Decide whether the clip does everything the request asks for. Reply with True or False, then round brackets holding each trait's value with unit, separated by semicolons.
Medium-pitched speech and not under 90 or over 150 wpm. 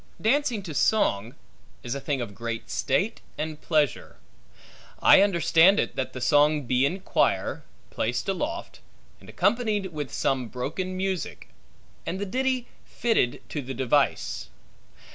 True (155 Hz; 140 wpm)